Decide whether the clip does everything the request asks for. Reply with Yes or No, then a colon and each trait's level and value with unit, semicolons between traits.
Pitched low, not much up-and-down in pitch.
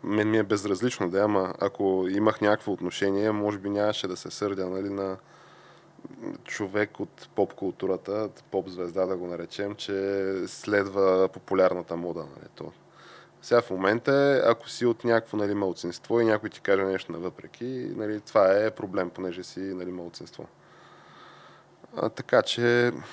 Yes: low, 100 Hz; narrow, 2.3 semitones